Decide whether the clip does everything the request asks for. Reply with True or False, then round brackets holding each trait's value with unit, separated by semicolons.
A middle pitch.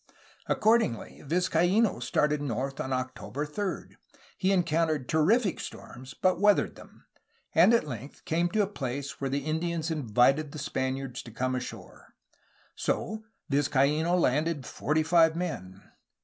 True (150 Hz)